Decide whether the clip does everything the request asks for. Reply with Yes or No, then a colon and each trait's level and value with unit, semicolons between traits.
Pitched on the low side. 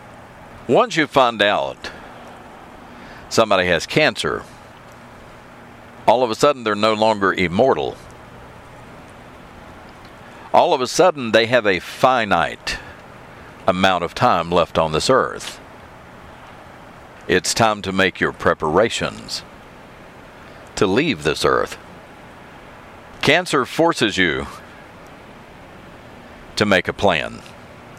Yes: low, 105 Hz